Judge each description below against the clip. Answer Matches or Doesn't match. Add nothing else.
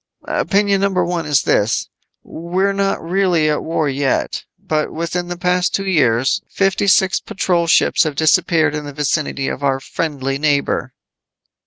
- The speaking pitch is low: Doesn't match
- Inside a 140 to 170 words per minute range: Matches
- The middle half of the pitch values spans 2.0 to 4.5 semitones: Matches